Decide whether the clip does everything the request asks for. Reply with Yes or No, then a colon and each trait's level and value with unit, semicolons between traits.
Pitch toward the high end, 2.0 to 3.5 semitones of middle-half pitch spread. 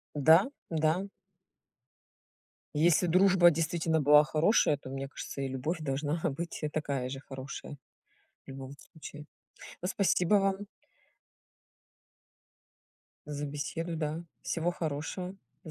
No: medium, 155 Hz; average, 3.1 semitones